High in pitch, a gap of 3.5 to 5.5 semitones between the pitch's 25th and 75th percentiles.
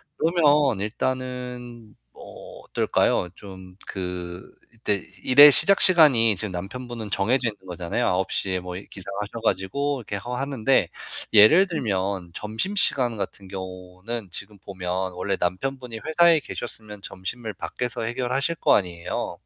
No: low, 110 Hz; average, 5.2 semitones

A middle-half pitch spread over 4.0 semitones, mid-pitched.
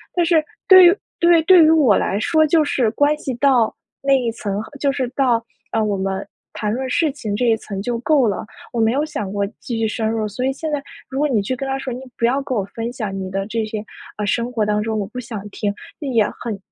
No: average, 4.7 semitones; high, 240 Hz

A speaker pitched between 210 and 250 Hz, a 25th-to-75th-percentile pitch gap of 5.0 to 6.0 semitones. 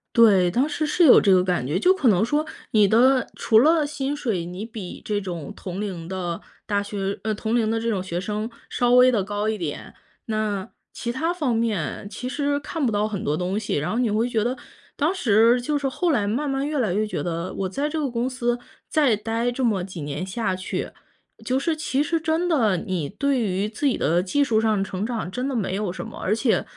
Yes: high, 220 Hz; average, 5.3 semitones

